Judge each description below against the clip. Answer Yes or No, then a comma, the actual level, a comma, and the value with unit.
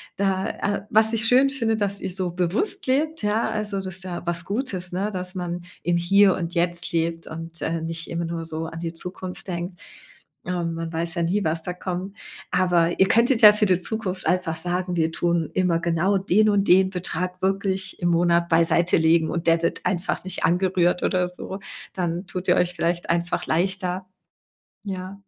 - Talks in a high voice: No, medium, 180 Hz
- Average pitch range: No, narrow, 2.3 semitones